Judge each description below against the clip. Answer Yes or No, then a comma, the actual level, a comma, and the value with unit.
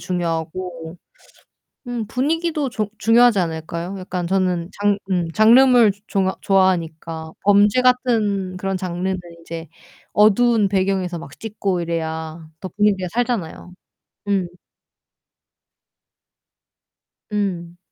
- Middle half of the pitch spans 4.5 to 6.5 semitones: No, average, 3.9 semitones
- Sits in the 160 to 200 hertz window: Yes, high, 190 Hz